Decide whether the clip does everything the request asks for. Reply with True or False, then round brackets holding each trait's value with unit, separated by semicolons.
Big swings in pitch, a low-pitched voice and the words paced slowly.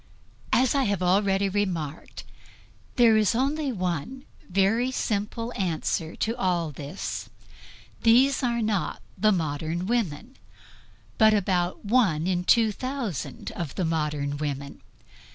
False (5.8 semitones; 195 Hz; 115 wpm)